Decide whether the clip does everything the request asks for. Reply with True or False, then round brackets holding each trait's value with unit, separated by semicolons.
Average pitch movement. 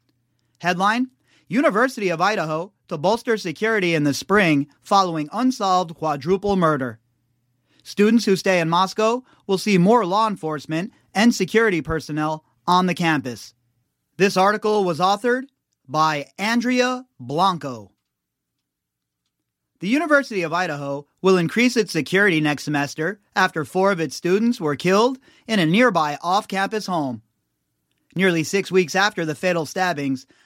False (5.8 semitones)